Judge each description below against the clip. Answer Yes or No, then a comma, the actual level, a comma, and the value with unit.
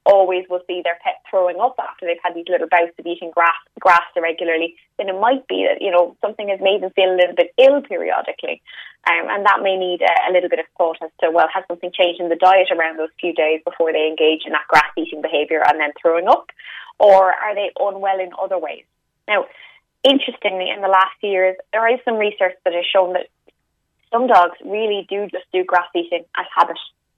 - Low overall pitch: No, medium, 180 Hz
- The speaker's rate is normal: No, fast, 225 wpm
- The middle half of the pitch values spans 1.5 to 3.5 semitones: Yes, narrow, 2.5 semitones